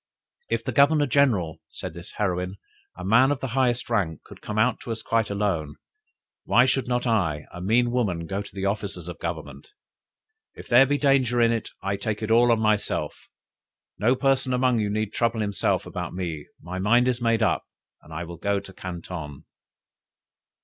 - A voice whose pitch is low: Yes, low, 105 Hz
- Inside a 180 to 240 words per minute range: Yes, average, 185 wpm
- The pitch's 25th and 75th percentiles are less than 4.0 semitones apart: No, average, 5.1 semitones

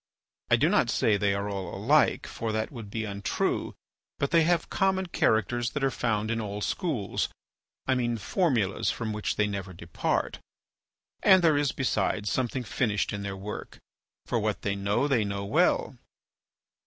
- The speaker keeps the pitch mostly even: No, average, 4.7 semitones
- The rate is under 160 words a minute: No, average, 165 wpm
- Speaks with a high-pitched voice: No, low, 110 Hz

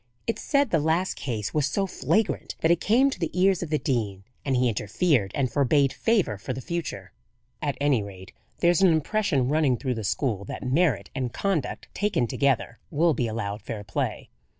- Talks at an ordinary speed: Yes, average, 195 wpm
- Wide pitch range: Yes, wide, 6.9 semitones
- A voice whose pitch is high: No, medium, 140 Hz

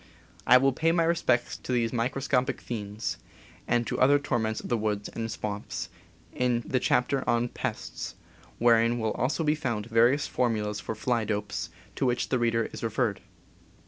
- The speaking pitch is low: Yes, low, 120 Hz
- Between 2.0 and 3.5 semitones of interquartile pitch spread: Yes, narrow, 2.5 semitones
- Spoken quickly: No, average, 175 wpm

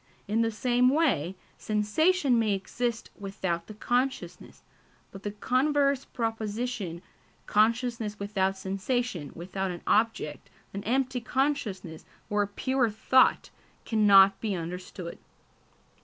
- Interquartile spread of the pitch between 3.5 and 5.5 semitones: Yes, average, 4.2 semitones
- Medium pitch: No, high, 215 Hz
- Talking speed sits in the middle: No, slow, 110 wpm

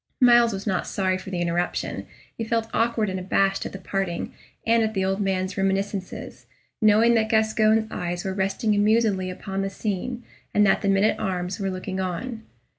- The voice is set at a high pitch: Yes, high, 195 Hz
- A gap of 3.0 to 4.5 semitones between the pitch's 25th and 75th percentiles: No, narrow, 2.6 semitones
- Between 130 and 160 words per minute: No, average, 190 wpm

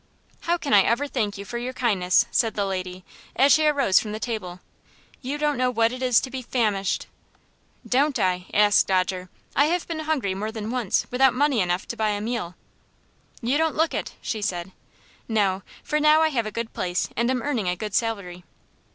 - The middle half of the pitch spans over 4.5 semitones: Yes, wide, 5.4 semitones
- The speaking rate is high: Yes, fast, 210 wpm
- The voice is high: Yes, high, 230 Hz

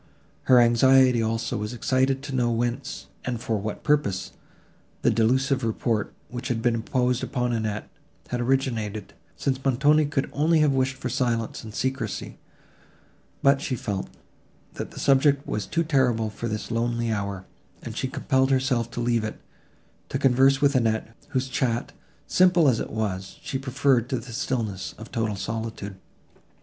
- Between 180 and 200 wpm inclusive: No, average, 160 wpm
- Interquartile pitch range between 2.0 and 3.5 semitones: Yes, average, 3.0 semitones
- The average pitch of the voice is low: Yes, low, 120 Hz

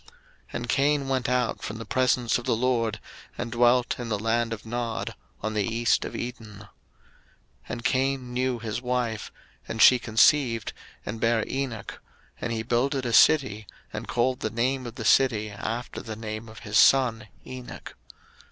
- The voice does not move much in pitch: Yes, narrow, 2.3 semitones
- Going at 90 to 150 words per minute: No, average, 175 wpm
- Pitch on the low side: Yes, low, 120 Hz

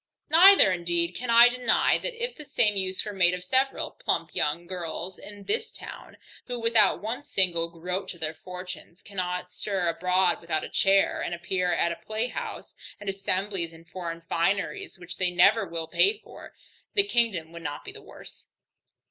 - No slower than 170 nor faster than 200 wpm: Yes, average, 180 wpm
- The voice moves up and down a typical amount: Yes, average, 4.4 semitones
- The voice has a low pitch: No, medium, 185 Hz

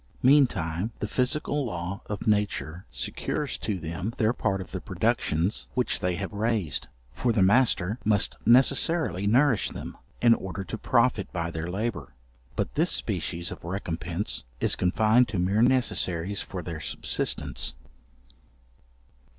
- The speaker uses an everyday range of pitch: Yes, average, 5.0 semitones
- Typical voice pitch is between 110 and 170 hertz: No, low, 100 Hz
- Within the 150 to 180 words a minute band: No, average, 140 wpm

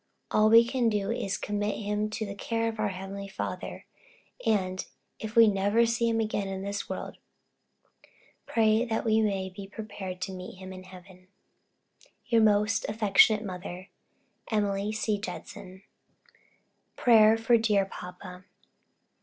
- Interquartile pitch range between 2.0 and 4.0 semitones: Yes, narrow, 2.4 semitones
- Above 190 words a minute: No, average, 145 wpm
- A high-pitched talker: Yes, high, 210 Hz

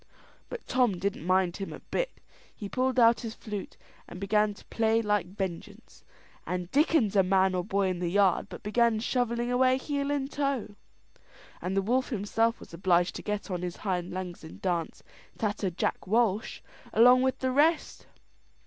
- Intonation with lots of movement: No, average, 4.7 semitones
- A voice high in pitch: Yes, high, 210 Hz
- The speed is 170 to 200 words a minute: Yes, average, 175 wpm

